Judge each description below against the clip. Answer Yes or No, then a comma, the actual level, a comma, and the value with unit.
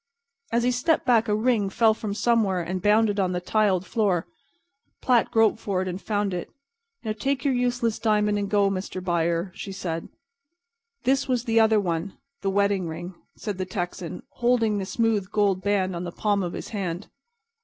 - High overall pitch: Yes, high, 205 Hz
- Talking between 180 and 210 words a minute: Yes, average, 185 wpm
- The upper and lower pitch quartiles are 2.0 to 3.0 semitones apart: No, average, 3.4 semitones